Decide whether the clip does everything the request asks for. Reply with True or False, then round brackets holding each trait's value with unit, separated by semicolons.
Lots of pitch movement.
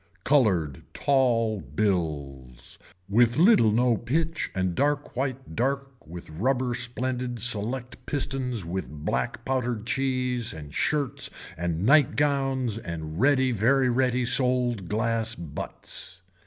True (5.7 semitones)